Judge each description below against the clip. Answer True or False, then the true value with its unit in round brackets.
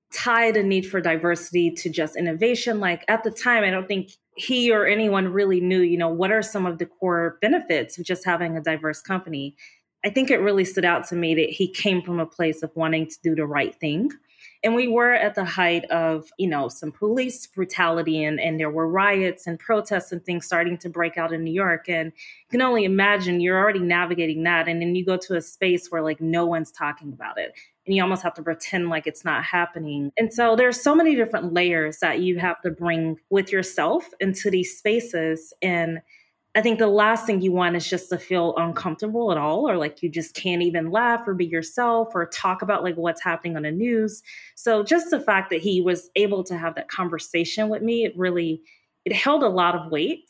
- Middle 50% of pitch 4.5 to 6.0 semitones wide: False (3.8 semitones)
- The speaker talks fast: True (225 wpm)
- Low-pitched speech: False (180 Hz)